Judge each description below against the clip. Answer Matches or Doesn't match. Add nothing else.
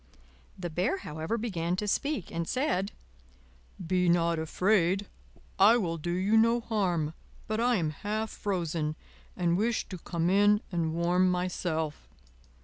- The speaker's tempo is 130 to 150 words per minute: Matches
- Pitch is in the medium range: Matches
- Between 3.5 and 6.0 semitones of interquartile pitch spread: Matches